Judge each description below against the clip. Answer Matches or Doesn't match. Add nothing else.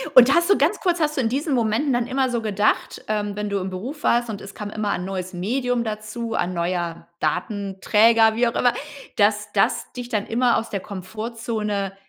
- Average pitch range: Matches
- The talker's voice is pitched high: Matches